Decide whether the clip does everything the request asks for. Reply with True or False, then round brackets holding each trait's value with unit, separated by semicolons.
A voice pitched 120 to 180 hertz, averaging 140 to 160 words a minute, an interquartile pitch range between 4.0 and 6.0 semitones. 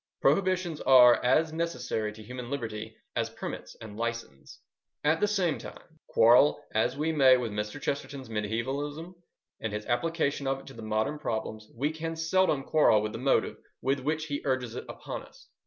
False (135 Hz; 170 wpm; 5.4 semitones)